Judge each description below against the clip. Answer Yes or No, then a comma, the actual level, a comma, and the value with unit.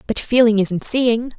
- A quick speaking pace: No, average, 175 wpm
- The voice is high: Yes, high, 225 Hz